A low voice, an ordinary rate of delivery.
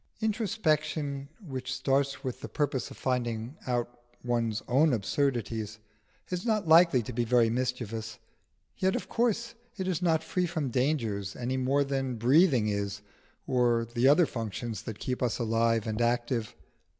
Yes: low, 125 Hz; average, 150 wpm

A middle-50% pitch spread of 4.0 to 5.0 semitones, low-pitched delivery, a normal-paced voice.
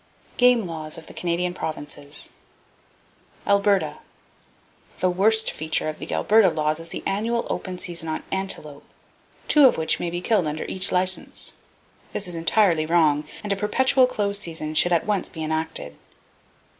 No: average, 4.4 semitones; medium, 175 Hz; average, 155 wpm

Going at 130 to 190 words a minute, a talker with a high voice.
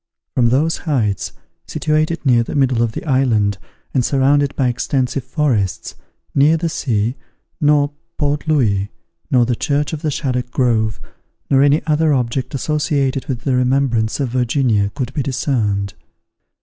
No: average, 150 wpm; low, 130 Hz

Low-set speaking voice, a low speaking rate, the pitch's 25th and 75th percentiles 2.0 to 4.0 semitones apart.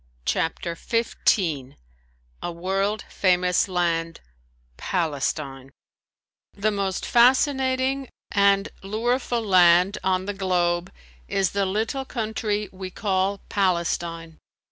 No: high, 190 Hz; slow, 95 wpm; average, 3.7 semitones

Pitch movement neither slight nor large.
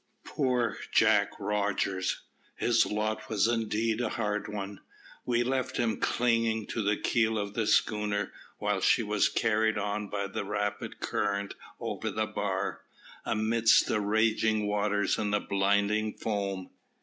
No: narrow, 1.6 semitones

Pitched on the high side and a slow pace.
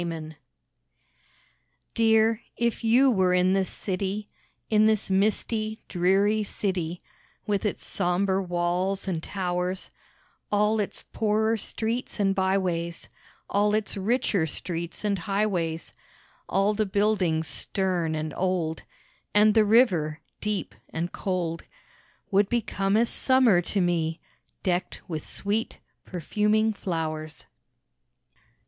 Yes: high, 195 Hz; slow, 115 wpm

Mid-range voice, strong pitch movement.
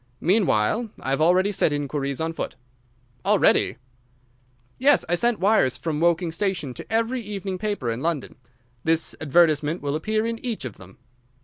Yes: medium, 170 Hz; wide, 6.2 semitones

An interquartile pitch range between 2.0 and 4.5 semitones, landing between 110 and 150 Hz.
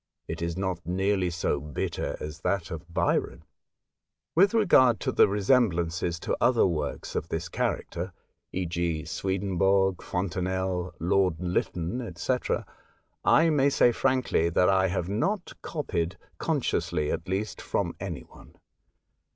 No: average, 3.2 semitones; very low, 90 Hz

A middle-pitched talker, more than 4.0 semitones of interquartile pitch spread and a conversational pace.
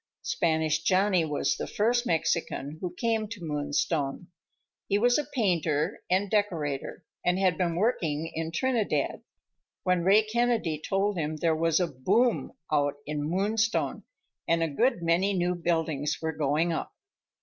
Yes: medium, 170 Hz; average, 4.6 semitones; average, 150 wpm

